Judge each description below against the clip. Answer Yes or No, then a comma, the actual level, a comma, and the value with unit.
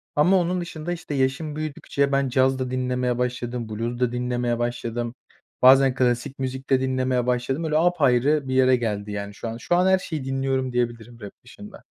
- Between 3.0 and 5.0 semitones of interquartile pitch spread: No, narrow, 2.6 semitones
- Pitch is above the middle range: No, low, 130 Hz